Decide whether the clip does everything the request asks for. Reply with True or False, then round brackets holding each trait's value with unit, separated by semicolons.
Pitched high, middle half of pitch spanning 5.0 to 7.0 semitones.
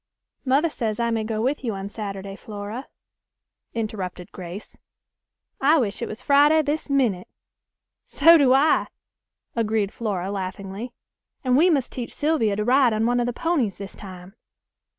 True (225 Hz; 5.4 semitones)